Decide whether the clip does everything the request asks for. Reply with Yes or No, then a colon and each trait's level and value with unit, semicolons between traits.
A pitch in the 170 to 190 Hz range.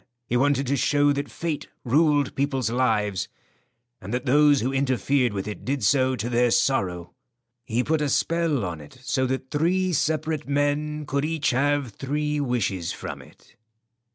No: low, 135 Hz